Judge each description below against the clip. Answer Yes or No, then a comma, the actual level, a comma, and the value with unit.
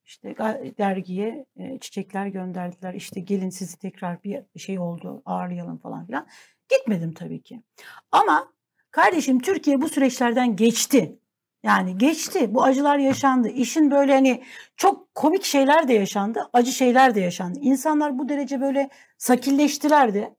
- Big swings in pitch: Yes, wide, 6.0 semitones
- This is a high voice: Yes, very high, 250 Hz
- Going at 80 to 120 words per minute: No, average, 135 wpm